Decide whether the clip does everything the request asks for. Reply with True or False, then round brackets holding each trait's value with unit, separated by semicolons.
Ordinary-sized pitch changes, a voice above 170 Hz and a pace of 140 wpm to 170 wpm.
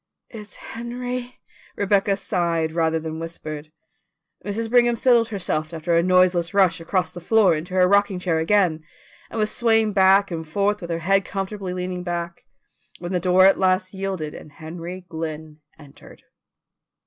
True (3.5 semitones; 185 Hz; 160 wpm)